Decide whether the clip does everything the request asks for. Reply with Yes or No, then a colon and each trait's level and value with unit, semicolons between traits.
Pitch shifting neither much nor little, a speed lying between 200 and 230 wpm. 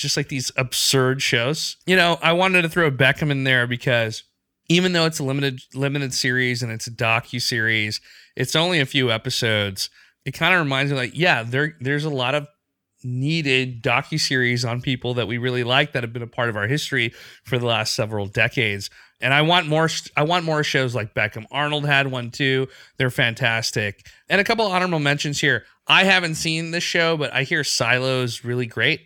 Yes: average, 3.9 semitones; fast, 205 wpm